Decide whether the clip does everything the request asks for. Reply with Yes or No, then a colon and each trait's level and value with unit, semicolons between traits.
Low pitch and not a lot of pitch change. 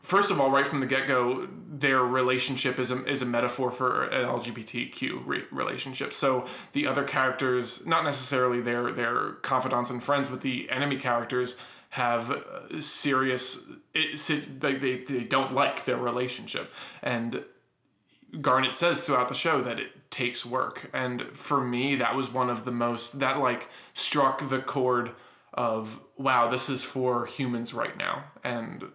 Yes: low, 130 Hz; narrow, 1.8 semitones